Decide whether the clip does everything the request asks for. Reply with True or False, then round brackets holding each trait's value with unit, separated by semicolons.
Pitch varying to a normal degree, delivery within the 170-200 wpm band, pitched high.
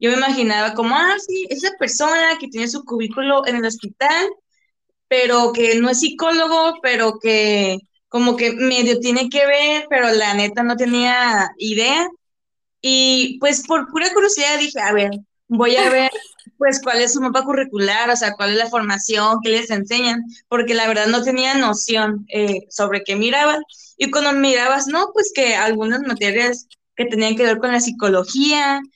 True (4.0 semitones; 175 wpm; 245 Hz)